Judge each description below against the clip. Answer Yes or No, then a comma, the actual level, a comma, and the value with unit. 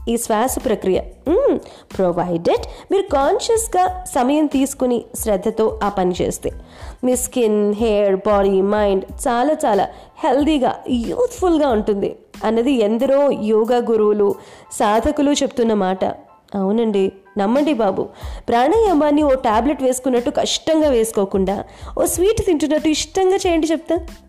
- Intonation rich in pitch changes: Yes, wide, 6.6 semitones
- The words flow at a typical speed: Yes, average, 110 wpm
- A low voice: No, very high, 255 Hz